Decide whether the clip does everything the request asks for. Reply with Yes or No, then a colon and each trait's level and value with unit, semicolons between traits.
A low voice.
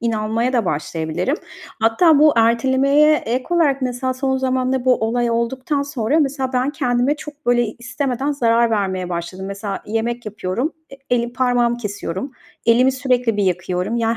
No: high, 245 Hz